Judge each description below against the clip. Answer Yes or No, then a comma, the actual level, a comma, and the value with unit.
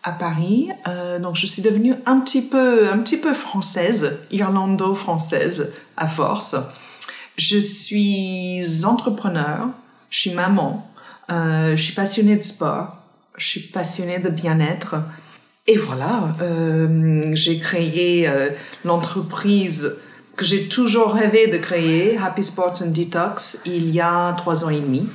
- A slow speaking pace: Yes, slow, 140 wpm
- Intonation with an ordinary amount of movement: Yes, average, 4.0 semitones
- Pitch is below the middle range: No, medium, 185 Hz